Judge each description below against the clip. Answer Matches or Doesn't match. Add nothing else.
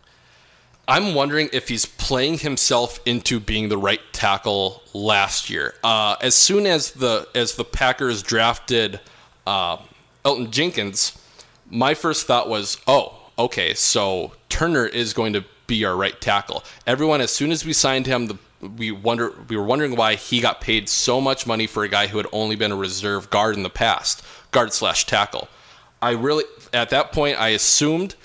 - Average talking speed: Matches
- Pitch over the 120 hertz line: Doesn't match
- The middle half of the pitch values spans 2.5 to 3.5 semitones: Doesn't match